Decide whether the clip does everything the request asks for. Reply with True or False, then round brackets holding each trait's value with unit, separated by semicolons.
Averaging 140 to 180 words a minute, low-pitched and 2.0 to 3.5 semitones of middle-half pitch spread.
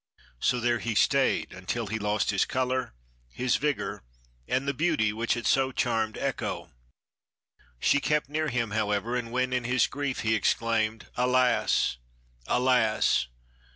True (145 wpm; 120 Hz; 2.9 semitones)